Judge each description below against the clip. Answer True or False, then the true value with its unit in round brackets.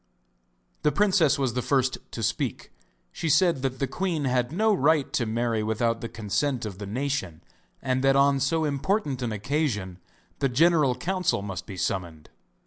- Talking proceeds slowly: False (170 wpm)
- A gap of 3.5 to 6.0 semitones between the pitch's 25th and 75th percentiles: True (4.9 semitones)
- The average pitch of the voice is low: True (130 Hz)